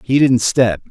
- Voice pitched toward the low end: Yes, low, 120 Hz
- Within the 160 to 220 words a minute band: Yes, average, 200 wpm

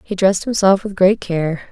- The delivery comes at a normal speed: No, fast, 210 wpm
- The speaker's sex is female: Yes, female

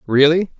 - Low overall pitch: No, medium, 155 Hz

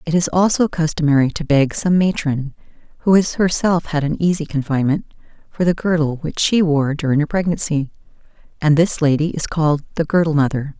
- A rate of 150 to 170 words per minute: No, average, 180 wpm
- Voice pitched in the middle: Yes, medium, 160 Hz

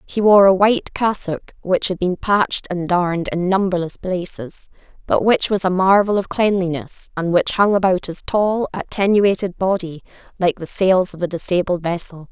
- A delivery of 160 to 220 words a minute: Yes, average, 175 wpm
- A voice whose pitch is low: No, medium, 185 Hz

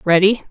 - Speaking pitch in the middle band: No, high, 195 Hz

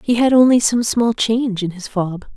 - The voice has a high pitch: Yes, high, 220 Hz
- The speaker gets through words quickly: Yes, fast, 230 wpm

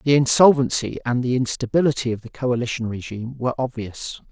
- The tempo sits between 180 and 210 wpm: No, average, 155 wpm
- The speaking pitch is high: No, low, 125 Hz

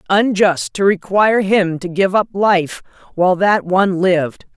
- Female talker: Yes, female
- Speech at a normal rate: Yes, average, 160 wpm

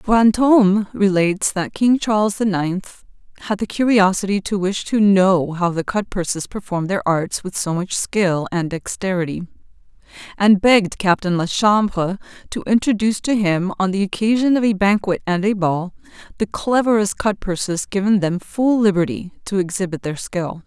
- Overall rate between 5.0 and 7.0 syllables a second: No, 4.8 syllables/s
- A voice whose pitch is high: Yes, high, 195 Hz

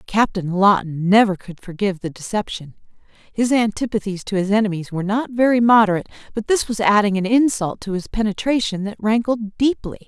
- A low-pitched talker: No, high, 205 Hz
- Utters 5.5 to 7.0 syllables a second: Yes, 5.7 syllables/s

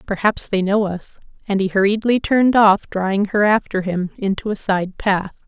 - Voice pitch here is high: Yes, high, 200 Hz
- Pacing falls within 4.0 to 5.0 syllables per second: Yes, 4.9 syllables/s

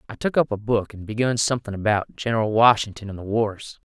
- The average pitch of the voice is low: Yes, low, 110 Hz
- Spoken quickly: Yes, fast, 215 wpm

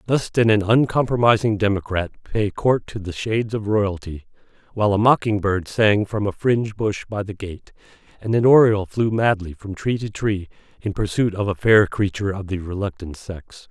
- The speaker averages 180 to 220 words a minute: Yes, average, 190 wpm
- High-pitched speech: No, low, 105 Hz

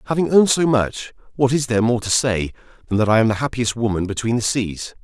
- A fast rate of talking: Yes, fast, 240 wpm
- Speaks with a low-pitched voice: Yes, low, 115 Hz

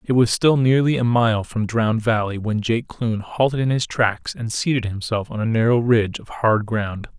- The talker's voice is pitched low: Yes, low, 115 Hz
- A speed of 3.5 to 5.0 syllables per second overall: Yes, 4.9 syllables/s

